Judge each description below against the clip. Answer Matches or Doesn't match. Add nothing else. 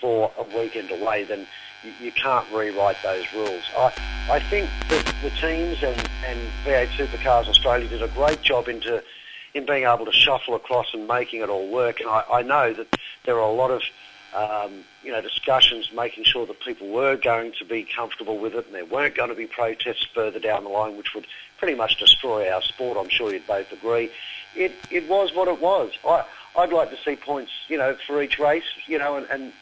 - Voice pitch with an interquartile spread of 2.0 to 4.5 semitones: Doesn't match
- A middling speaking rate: Doesn't match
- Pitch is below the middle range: Matches